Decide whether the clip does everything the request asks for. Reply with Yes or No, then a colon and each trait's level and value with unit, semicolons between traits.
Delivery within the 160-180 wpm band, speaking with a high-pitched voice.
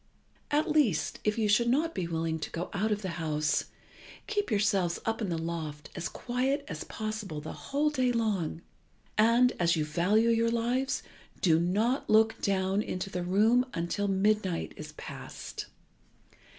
Yes: average, 165 wpm; high, 205 Hz